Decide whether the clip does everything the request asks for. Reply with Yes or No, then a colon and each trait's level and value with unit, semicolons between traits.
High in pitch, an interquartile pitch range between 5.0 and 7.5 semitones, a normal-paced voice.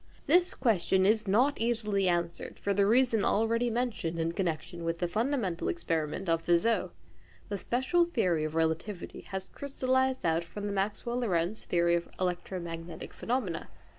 Yes: high, 195 Hz; wide, 5.6 semitones; average, 150 wpm